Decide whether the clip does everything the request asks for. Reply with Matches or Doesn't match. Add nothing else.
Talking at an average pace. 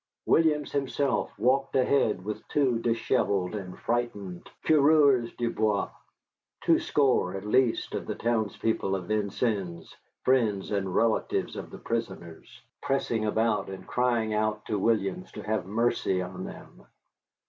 Doesn't match